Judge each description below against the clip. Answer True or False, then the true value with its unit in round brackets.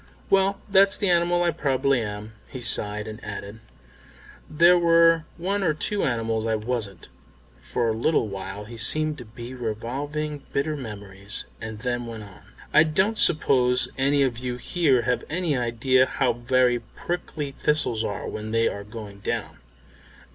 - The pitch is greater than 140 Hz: False (125 Hz)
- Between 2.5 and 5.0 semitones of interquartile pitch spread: False (5.6 semitones)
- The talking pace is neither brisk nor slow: True (160 wpm)